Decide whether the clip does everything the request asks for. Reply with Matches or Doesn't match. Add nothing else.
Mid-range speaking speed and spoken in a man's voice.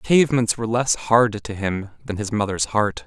Doesn't match